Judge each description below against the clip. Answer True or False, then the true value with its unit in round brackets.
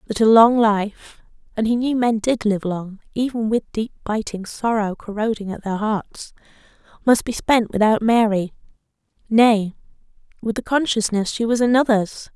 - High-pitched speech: True (220 Hz)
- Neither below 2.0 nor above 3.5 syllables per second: True (3.2 syllables/s)